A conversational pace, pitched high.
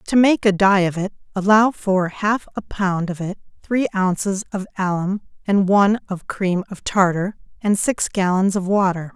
Yes: average, 185 wpm; high, 195 Hz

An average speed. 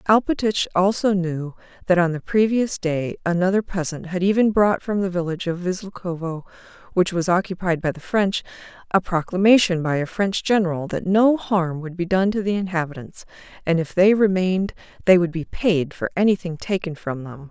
Yes: average, 180 wpm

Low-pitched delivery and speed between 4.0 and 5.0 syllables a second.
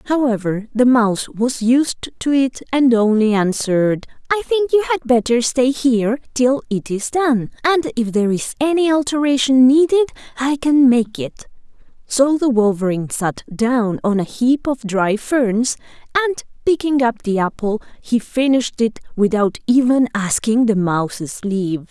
No: high, 245 Hz; 4.5 syllables/s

